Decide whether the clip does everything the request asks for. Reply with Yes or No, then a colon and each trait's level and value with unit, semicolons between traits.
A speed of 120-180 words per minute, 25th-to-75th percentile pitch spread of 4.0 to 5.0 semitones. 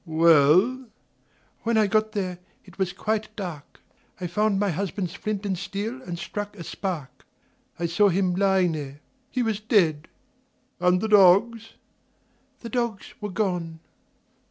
No: average, 150 wpm; average, 3.4 semitones